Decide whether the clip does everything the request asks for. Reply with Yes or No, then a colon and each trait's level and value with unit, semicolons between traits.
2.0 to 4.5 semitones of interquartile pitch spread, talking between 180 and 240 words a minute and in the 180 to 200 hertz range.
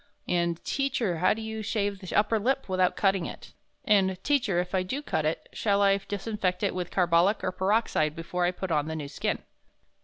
Yes: average, 3.1 semitones; fast, 205 wpm; high, 190 Hz